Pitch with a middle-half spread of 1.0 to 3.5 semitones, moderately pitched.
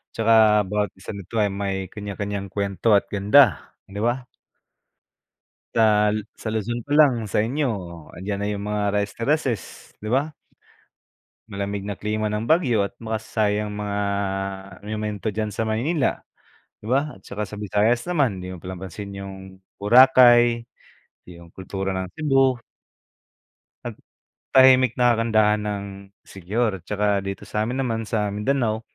No: average, 2.8 semitones; low, 105 Hz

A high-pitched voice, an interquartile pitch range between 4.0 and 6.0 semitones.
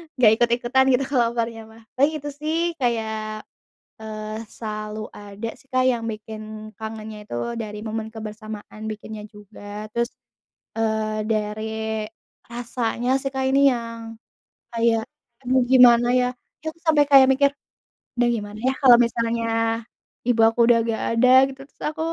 No: high, 230 Hz; narrow, 2.5 semitones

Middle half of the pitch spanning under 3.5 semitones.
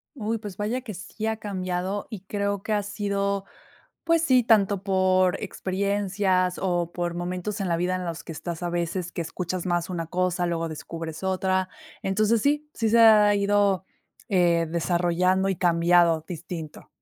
Yes: average, 2.8 semitones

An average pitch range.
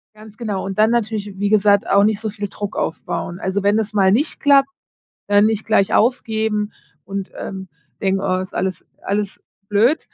No: narrow, 1.9 semitones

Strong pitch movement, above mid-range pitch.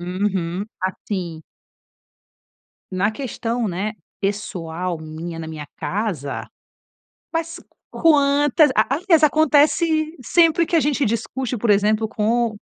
Yes: wide, 8.1 semitones; high, 220 Hz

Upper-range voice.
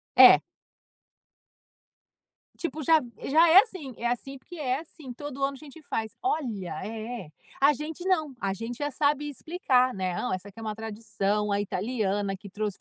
Yes: very high, 250 Hz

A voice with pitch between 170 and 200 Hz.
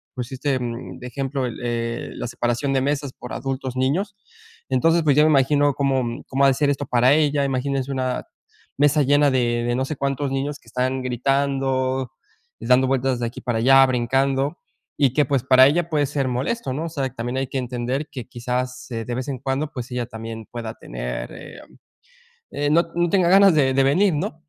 No: low, 135 Hz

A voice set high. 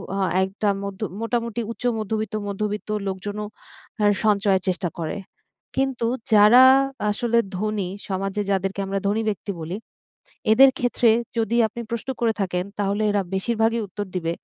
Yes: high, 210 Hz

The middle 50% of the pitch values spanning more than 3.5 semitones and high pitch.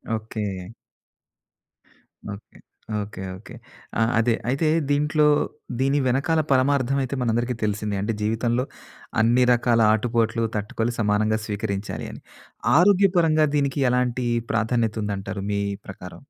No: average, 3.9 semitones; low, 115 Hz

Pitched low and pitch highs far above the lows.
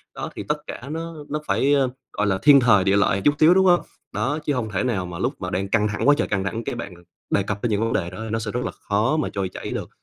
Yes: low, 115 Hz; wide, 6.3 semitones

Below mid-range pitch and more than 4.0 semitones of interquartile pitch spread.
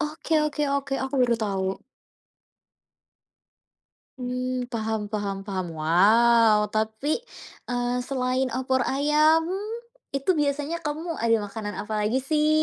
No: very high, 250 Hz; average, 5.0 semitones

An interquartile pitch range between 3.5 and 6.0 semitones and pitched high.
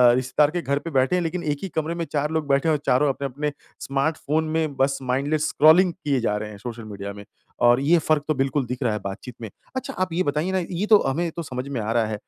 No: average, 4.1 semitones; medium, 145 Hz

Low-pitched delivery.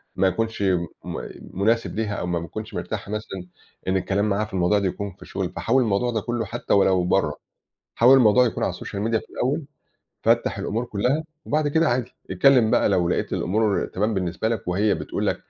Yes: low, 105 Hz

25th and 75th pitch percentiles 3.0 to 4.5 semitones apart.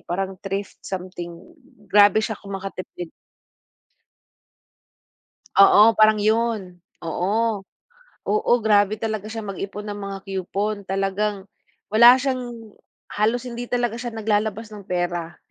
No: narrow, 2.4 semitones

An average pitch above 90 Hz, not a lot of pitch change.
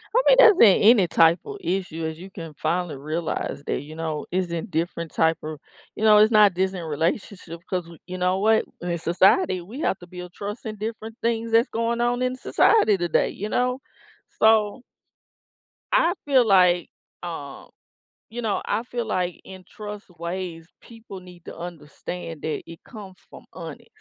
No: medium, 185 Hz; average, 4.7 semitones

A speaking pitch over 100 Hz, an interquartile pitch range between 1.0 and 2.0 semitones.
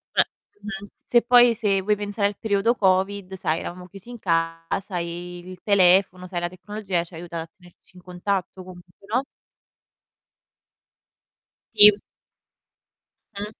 No: high, 190 Hz; narrow, 2.6 semitones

